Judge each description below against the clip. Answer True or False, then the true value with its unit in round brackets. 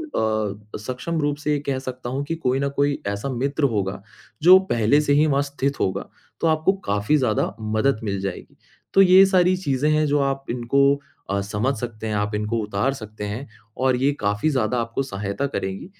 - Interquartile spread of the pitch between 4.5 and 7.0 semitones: True (5.1 semitones)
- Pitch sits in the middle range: False (130 Hz)